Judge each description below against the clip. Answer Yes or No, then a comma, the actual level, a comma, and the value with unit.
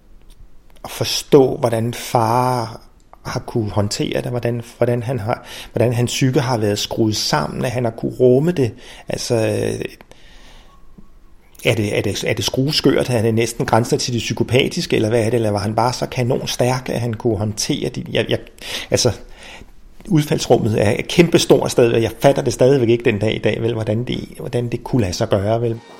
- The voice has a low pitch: Yes, low, 120 Hz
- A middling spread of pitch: No, narrow, 2.2 semitones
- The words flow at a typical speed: Yes, average, 190 wpm